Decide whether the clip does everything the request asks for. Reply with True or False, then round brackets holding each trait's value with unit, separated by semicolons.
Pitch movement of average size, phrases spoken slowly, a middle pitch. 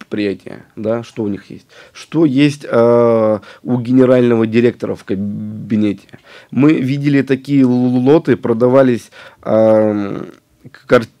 False (3.5 semitones; 105 wpm; 120 Hz)